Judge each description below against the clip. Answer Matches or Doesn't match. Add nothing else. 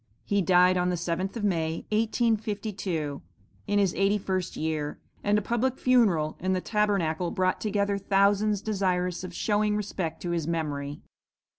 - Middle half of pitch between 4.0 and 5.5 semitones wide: Doesn't match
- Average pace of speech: Matches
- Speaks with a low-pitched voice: Doesn't match